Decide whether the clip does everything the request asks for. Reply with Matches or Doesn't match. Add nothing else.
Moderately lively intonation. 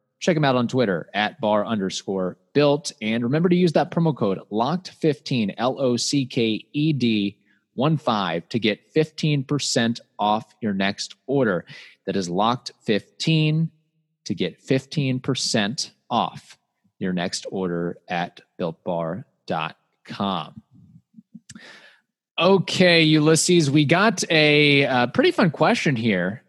Doesn't match